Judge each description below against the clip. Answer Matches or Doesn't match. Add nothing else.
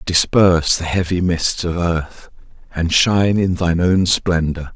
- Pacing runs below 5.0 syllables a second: Matches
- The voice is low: Matches